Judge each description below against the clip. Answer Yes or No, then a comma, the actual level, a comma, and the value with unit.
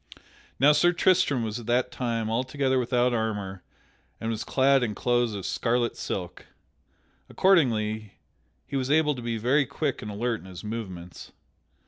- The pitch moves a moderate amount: Yes, average, 3.8 semitones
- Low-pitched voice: Yes, low, 120 Hz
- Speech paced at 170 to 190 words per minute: No, average, 155 wpm